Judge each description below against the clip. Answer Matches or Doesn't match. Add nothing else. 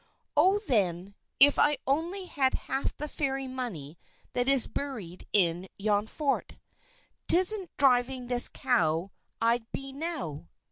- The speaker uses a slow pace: Matches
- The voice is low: Doesn't match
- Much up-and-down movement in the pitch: Matches